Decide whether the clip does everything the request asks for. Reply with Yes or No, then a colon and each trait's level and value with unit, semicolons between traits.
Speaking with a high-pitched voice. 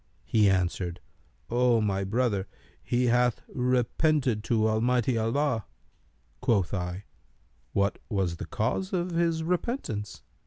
No: low, 115 Hz